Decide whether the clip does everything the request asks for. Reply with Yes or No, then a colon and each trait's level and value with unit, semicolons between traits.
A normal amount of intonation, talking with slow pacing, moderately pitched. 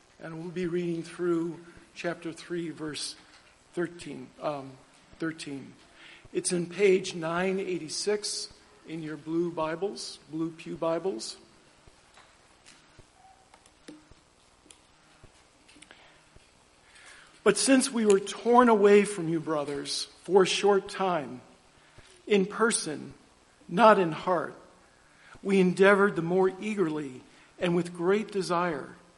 Yes: average, 3.7 semitones; slow, 105 wpm; medium, 175 Hz